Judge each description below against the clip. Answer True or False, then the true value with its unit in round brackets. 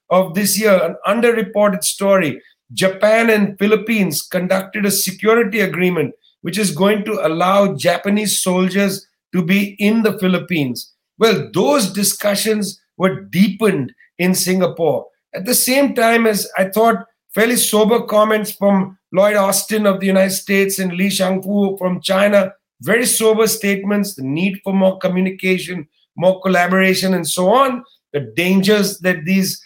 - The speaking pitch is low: False (195 Hz)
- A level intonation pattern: True (2.3 semitones)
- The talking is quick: False (145 wpm)